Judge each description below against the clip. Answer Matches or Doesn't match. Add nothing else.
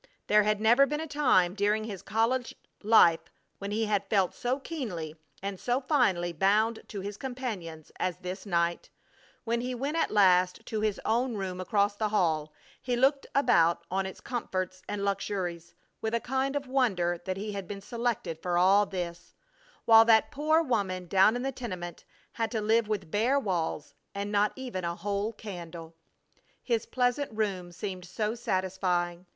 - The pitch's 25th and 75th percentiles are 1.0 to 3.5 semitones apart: Doesn't match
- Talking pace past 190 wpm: Doesn't match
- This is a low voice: Doesn't match